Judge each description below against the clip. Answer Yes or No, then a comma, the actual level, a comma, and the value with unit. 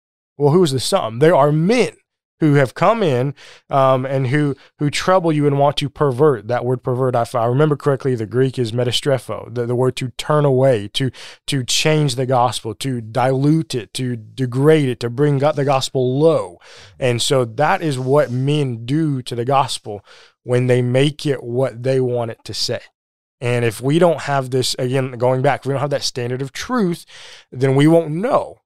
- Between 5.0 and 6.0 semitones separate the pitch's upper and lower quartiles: No, average, 2.8 semitones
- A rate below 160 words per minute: No, average, 200 wpm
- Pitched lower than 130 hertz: No, low, 135 Hz